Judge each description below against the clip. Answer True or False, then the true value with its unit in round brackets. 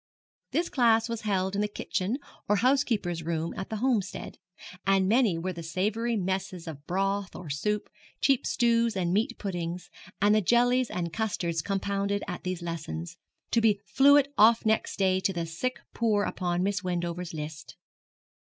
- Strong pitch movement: False (4.1 semitones)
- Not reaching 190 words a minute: True (165 wpm)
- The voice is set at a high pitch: True (195 Hz)